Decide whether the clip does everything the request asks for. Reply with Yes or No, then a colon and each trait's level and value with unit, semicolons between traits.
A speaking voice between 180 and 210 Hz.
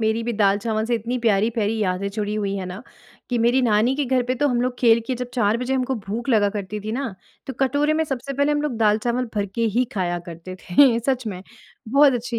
No: high, 230 Hz